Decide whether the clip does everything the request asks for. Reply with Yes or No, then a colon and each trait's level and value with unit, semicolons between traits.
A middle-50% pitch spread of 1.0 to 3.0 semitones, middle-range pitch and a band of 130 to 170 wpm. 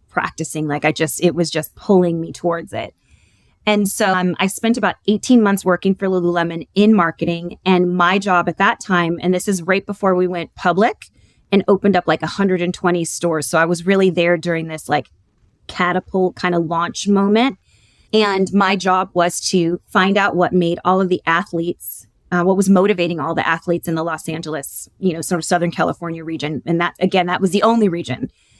No: narrow, 2.5 semitones; medium, 175 Hz; average, 200 wpm